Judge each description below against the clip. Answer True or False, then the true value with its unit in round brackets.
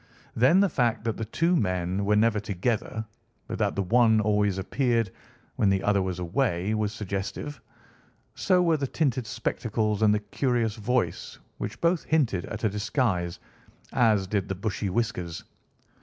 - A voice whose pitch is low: True (110 Hz)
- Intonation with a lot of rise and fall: False (3.6 semitones)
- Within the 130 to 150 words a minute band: False (160 wpm)